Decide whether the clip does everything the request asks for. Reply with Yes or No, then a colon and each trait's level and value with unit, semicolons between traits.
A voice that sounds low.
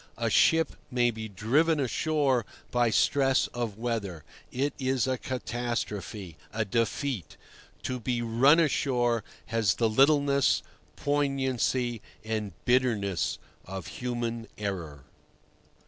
Yes: low, 120 Hz